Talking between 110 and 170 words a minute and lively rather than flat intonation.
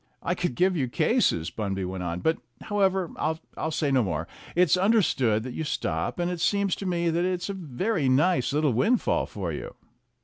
No: average, 195 wpm; wide, 7.0 semitones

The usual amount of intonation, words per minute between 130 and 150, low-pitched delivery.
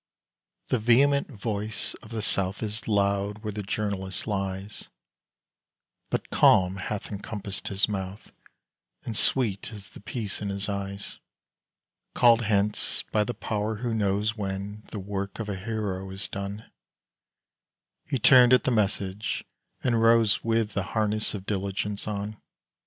No: narrow, 1.9 semitones; average, 140 wpm; low, 105 Hz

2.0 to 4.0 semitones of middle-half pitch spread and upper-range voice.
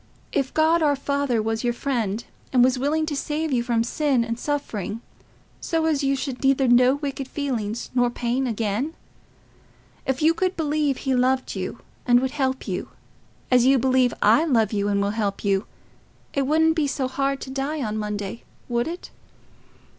Yes: average, 3.5 semitones; very high, 260 Hz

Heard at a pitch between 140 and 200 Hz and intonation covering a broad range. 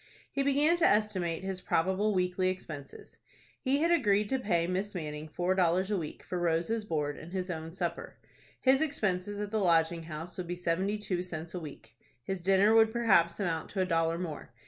No: medium, 185 Hz; average, 3.8 semitones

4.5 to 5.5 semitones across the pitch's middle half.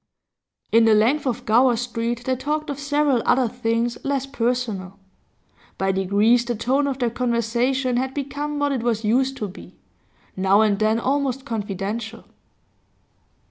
No: average, 3.3 semitones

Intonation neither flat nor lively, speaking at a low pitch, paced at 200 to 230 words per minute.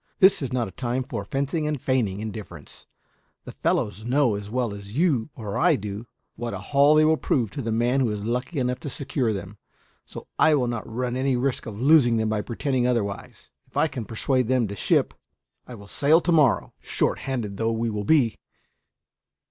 Yes: average, 4.0 semitones; low, 120 Hz; fast, 205 wpm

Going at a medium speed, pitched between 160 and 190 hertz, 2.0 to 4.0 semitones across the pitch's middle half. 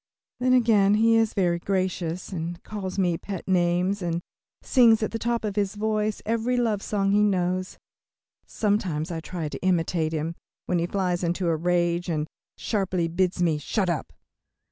Yes: average, 170 wpm; medium, 185 Hz; average, 3.3 semitones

